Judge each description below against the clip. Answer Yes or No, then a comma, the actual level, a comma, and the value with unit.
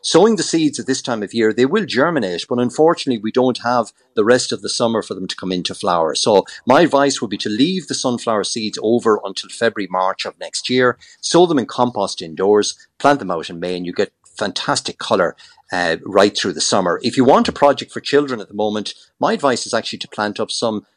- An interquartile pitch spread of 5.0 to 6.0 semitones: No, average, 4.1 semitones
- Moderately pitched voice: No, low, 120 Hz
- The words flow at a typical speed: No, fast, 235 wpm